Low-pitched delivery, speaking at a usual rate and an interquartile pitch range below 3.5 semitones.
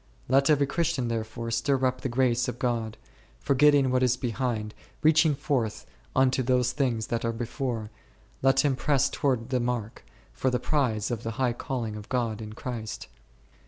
Yes: low, 125 Hz; average, 170 wpm; narrow, 2.6 semitones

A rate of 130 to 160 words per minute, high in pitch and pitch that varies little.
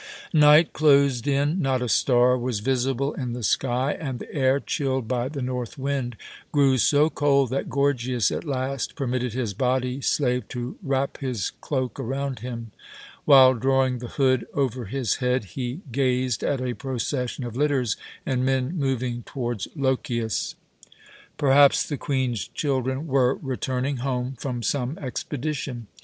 No: average, 150 wpm; low, 130 Hz; narrow, 2.0 semitones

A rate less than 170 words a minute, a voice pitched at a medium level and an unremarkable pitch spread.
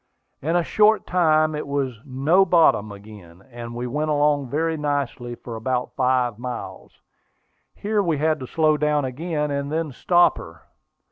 Yes: average, 160 wpm; medium, 145 Hz; average, 4.3 semitones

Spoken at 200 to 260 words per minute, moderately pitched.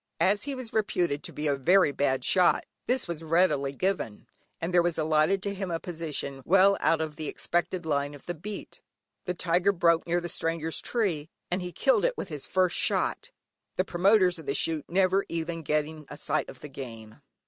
Yes: fast, 205 wpm; medium, 170 Hz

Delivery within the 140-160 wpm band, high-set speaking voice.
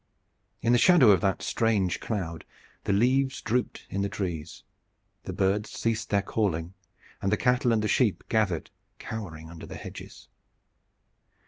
No: average, 150 wpm; low, 105 Hz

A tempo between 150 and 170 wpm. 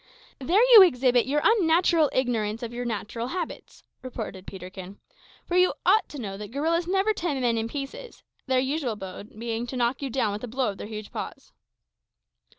No: average, 190 wpm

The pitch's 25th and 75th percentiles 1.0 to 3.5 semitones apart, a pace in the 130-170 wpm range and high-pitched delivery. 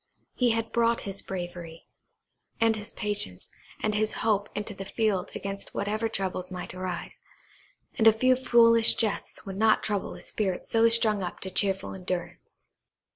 Yes: average, 3.1 semitones; average, 160 wpm; high, 210 Hz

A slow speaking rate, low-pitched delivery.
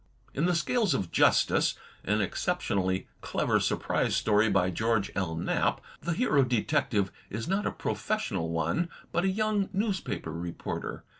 No: average, 150 wpm; low, 110 Hz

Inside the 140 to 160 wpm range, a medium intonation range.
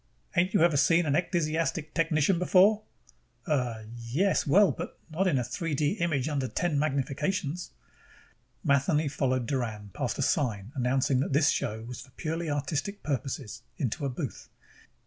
Yes: average, 155 wpm; average, 4.6 semitones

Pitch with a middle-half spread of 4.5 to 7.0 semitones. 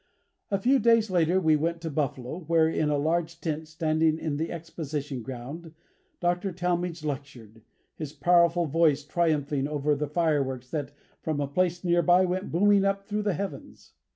No: average, 3.1 semitones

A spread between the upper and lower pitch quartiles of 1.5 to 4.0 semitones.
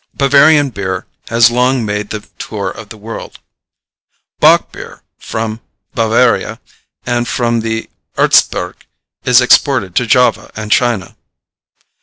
Yes: narrow, 2.6 semitones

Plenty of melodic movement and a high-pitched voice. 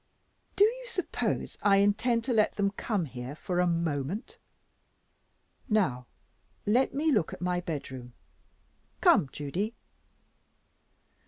Yes: wide, 7.3 semitones; high, 195 Hz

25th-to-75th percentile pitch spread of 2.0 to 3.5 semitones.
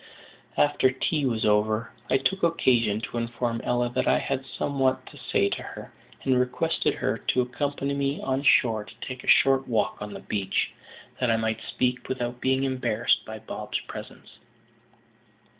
Yes: average, 2.8 semitones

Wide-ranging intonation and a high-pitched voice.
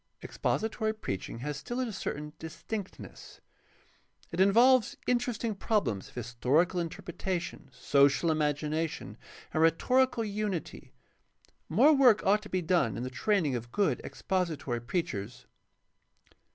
No: wide, 6.8 semitones; medium, 175 Hz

